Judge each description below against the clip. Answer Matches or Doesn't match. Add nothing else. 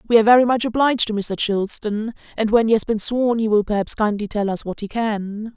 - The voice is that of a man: Doesn't match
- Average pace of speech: Doesn't match